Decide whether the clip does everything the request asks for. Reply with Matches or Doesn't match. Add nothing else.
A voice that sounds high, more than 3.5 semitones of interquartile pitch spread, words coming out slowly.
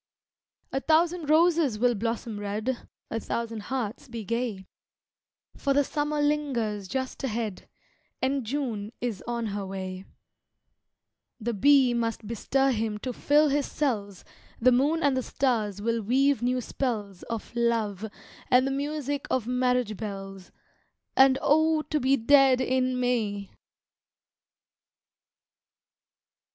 Matches